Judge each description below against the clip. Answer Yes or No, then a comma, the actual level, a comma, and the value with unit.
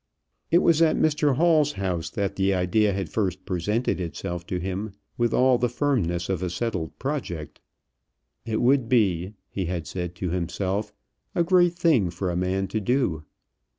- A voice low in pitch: Yes, low, 100 Hz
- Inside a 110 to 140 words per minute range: No, average, 170 wpm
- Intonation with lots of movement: Yes, wide, 6.1 semitones